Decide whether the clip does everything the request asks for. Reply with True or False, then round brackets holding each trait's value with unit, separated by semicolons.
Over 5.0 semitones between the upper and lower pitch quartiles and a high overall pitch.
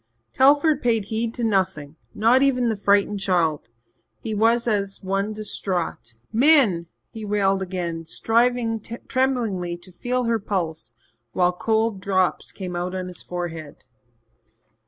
False (4.4 semitones; 200 Hz)